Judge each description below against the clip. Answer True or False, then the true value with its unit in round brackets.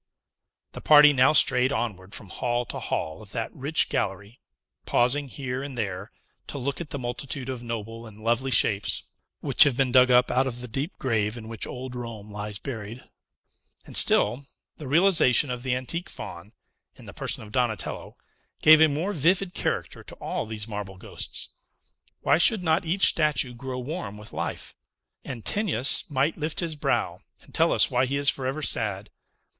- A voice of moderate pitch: False (125 Hz)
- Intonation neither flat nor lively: True (4.4 semitones)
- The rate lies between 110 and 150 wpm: False (180 wpm)